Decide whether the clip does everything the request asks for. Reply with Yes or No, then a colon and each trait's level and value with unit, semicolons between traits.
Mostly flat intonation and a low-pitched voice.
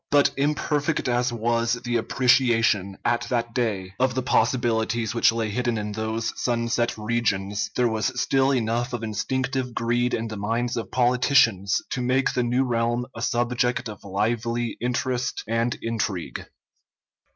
Yes: narrow, 1.8 semitones; low, 120 Hz